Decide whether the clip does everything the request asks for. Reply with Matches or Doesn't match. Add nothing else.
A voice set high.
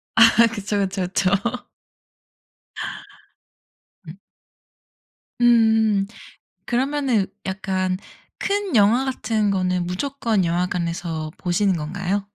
Matches